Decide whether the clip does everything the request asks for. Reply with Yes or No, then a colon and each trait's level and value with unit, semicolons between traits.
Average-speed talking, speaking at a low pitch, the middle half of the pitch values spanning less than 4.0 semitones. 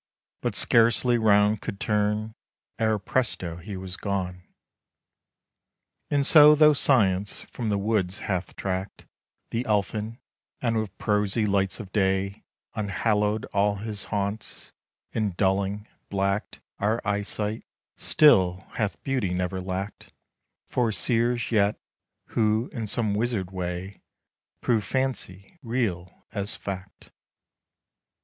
No: slow, 115 wpm; low, 105 Hz; average, 2.7 semitones